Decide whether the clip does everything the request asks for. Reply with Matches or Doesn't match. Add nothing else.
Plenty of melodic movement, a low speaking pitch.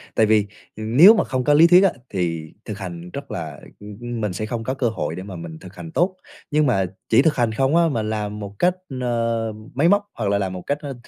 Matches